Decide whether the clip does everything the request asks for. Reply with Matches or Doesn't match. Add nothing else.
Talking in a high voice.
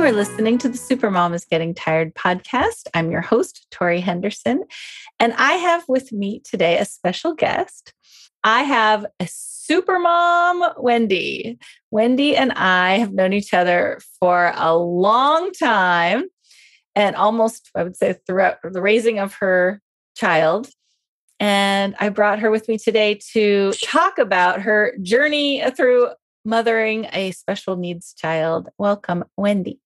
Matches